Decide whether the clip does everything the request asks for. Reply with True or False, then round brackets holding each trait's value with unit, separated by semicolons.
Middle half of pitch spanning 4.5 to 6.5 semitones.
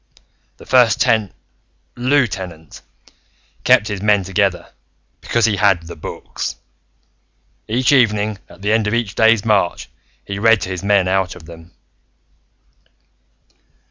False (3.0 semitones)